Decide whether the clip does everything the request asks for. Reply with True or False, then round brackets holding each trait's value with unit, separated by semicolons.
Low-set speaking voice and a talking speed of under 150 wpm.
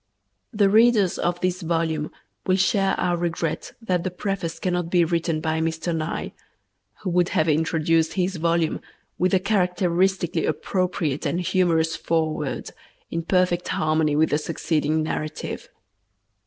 False (170 Hz; 140 wpm)